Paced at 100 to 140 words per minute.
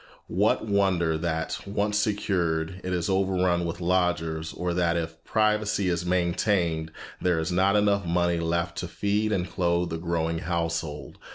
No: average, 155 wpm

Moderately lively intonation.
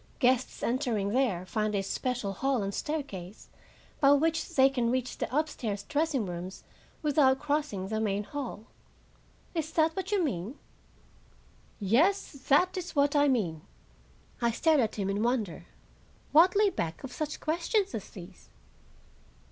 No: wide, 6.9 semitones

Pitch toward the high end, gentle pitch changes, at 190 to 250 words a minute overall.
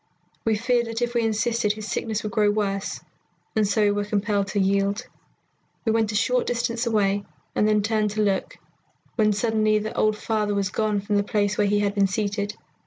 Yes: high, 210 Hz; narrow, 1.5 semitones; fast, 205 wpm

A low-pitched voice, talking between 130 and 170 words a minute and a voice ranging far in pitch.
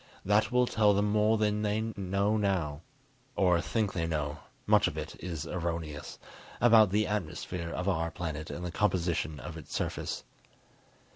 No: very low, 95 Hz; average, 160 wpm; average, 4.2 semitones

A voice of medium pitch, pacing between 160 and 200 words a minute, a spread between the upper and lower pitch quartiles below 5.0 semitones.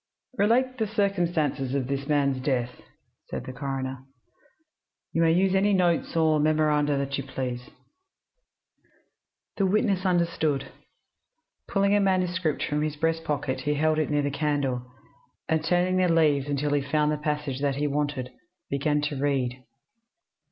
No: medium, 150 Hz; average, 150 wpm; average, 3.7 semitones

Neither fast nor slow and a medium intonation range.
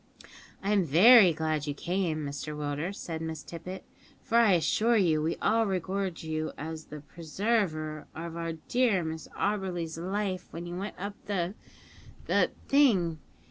Yes: average, 150 wpm; average, 3.9 semitones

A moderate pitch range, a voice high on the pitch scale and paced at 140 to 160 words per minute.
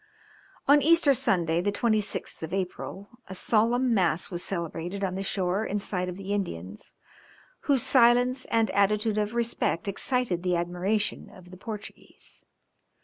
Yes: average, 4.4 semitones; high, 200 Hz; average, 145 wpm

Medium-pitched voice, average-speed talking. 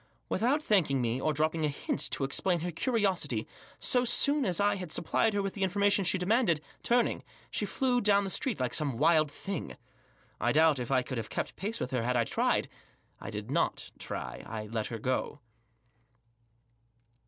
Yes: medium, 170 Hz; average, 190 wpm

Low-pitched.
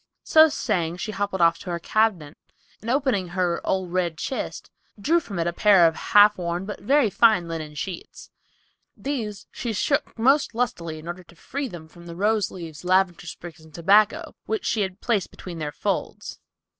No: medium, 185 Hz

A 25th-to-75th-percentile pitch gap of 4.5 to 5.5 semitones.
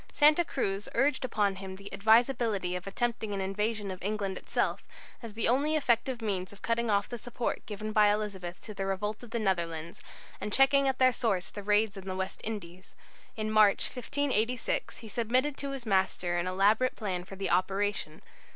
No: average, 3.6 semitones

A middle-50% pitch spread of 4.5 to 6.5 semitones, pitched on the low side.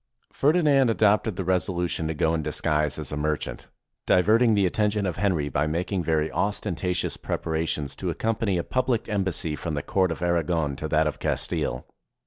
Yes: average, 4.9 semitones; very low, 90 Hz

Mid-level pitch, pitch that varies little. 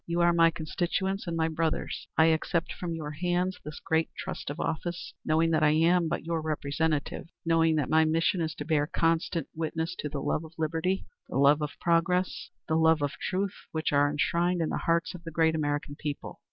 Yes: medium, 160 Hz; narrow, 1.6 semitones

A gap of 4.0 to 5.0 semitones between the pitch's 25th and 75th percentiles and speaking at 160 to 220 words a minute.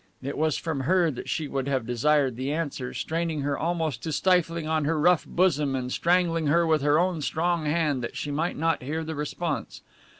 No: average, 3.0 semitones; fast, 205 wpm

